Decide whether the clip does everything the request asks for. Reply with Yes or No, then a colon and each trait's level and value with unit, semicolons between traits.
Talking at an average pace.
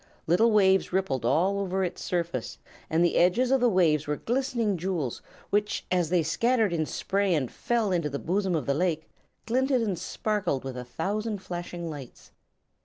Yes: average, 180 wpm